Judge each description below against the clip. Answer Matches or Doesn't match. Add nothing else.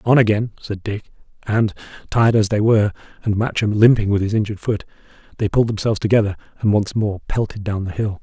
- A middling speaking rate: Matches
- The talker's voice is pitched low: Matches